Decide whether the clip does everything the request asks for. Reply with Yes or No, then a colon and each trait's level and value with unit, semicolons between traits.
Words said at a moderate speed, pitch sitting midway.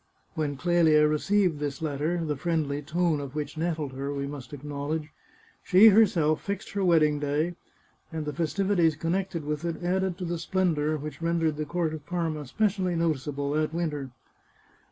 Yes: average, 175 wpm; medium, 155 Hz